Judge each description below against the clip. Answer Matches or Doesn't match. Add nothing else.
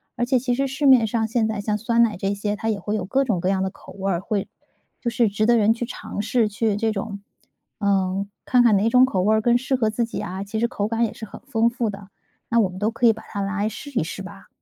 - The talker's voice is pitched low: Doesn't match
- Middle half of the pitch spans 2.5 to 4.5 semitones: Matches